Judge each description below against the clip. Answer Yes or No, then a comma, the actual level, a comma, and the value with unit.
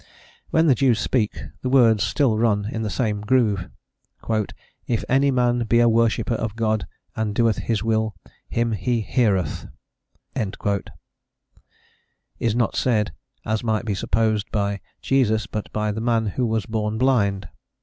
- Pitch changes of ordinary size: No, narrow, 2.1 semitones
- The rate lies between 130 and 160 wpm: Yes, average, 150 wpm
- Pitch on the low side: Yes, low, 110 Hz